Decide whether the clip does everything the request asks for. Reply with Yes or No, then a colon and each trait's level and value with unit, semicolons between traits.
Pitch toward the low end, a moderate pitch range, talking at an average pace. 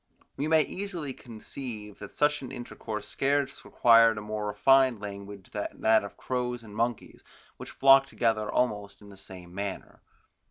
Yes: low, 115 Hz; average, 4.4 semitones; average, 160 wpm